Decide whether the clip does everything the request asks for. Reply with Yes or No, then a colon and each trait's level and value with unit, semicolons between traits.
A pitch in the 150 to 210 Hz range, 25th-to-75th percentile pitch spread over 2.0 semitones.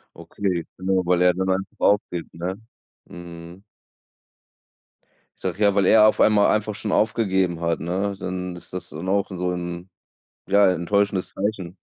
No: very low, 95 Hz; narrow, 2.4 semitones